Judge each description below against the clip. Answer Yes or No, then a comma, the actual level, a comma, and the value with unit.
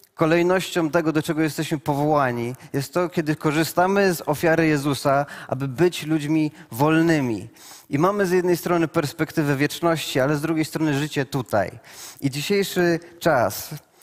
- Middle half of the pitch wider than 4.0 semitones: No, average, 2.7 semitones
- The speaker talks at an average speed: Yes, average, 140 wpm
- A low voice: No, medium, 160 Hz